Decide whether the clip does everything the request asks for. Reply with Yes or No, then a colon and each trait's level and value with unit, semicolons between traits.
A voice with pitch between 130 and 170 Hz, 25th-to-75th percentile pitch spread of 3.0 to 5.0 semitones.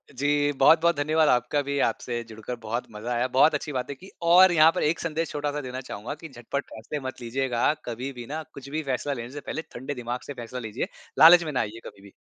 Yes: low, 135 Hz; average, 3.7 semitones